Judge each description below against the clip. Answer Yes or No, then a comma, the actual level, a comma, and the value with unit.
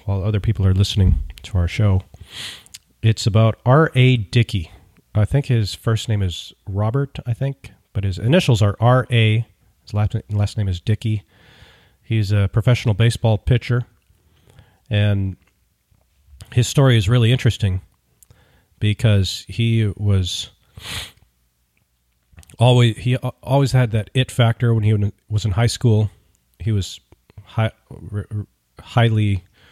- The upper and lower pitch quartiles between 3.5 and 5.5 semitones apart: No, average, 3.1 semitones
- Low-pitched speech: Yes, low, 105 Hz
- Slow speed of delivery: Yes, slow, 130 wpm